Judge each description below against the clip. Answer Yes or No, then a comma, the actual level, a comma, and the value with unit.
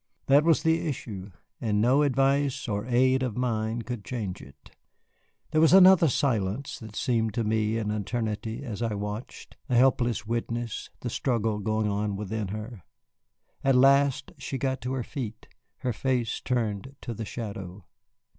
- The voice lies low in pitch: Yes, low, 115 Hz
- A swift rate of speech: No, average, 160 wpm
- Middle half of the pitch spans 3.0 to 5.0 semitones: Yes, average, 3.8 semitones